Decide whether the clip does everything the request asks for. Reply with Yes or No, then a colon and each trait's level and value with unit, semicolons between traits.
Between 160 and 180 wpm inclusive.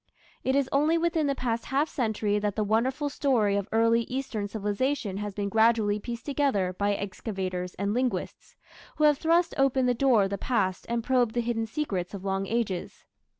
No: average, 190 wpm